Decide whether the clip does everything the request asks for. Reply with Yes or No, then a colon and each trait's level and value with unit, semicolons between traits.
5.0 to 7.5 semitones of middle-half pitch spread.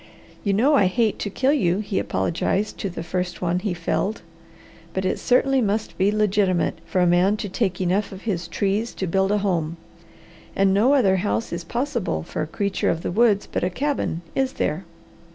No: average, 3.3 semitones